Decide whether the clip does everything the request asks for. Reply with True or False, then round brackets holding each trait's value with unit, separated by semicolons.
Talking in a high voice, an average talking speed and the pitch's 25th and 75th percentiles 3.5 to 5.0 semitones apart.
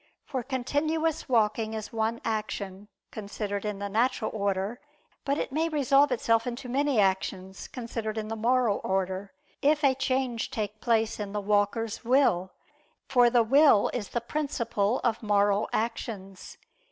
True (225 Hz; 150 wpm; 3.9 semitones)